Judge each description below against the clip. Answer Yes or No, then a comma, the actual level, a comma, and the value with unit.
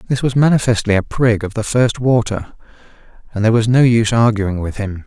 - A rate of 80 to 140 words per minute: No, average, 200 wpm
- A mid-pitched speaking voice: No, low, 115 Hz